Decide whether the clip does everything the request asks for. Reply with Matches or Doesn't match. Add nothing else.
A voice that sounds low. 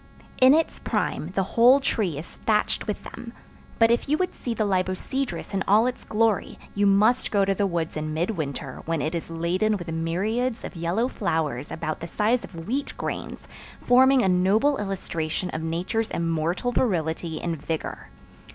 Doesn't match